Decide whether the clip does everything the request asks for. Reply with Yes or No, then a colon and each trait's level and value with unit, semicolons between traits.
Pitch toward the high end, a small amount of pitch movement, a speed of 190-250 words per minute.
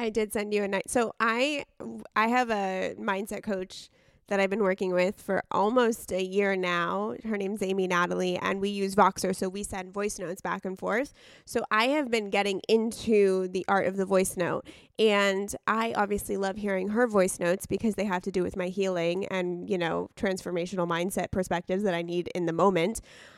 Yes: high, 195 Hz; narrow, 2.1 semitones; fast, 205 wpm